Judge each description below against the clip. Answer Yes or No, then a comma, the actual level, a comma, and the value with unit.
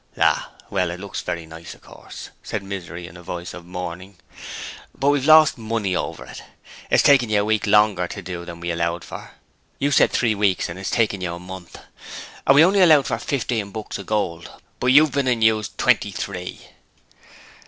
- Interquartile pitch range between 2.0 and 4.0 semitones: No, average, 4.8 semitones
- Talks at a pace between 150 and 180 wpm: No, average, 200 wpm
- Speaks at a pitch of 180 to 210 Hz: No, low, 100 Hz